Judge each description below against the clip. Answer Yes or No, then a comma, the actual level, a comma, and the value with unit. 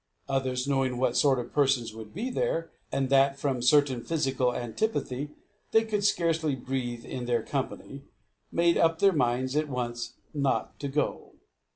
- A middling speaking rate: Yes, average, 165 wpm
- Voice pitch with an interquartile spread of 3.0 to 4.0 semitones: Yes, average, 3.4 semitones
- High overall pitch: No, low, 135 Hz